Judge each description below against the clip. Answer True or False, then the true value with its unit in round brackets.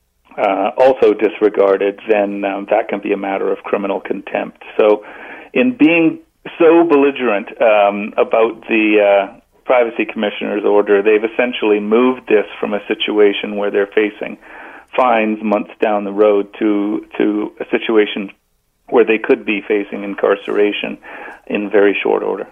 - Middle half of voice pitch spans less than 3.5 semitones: True (3.1 semitones)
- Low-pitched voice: True (105 Hz)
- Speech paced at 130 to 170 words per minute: True (145 wpm)